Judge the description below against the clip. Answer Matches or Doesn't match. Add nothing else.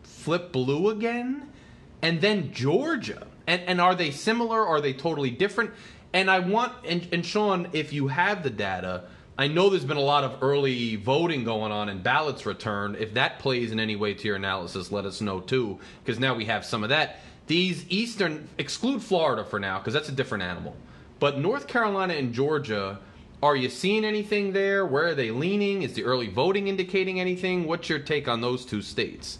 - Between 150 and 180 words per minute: Doesn't match